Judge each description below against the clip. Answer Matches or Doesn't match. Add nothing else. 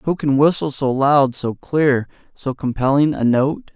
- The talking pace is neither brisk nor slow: Matches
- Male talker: Matches